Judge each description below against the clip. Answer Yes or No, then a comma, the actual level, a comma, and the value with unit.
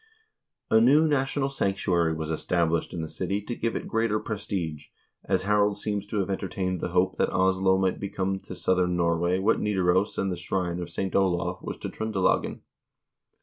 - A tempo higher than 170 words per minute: Yes, average, 180 wpm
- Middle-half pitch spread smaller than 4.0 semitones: Yes, average, 2.7 semitones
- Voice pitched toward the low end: Yes, very low, 95 Hz